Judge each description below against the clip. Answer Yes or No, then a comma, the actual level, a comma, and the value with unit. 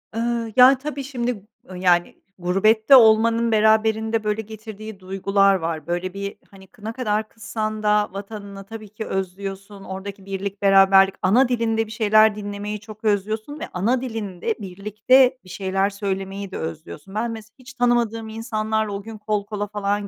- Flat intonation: Yes, narrow, 2.2 semitones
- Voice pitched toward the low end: No, high, 210 Hz